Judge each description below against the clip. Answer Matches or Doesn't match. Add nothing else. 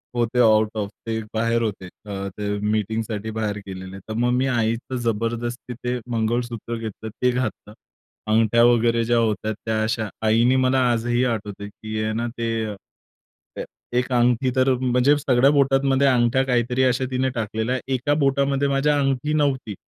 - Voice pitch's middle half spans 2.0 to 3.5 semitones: Matches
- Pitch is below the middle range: Matches